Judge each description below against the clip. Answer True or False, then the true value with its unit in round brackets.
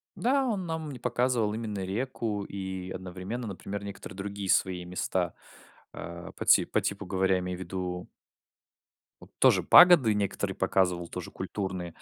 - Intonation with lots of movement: False (4.1 semitones)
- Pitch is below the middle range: True (100 Hz)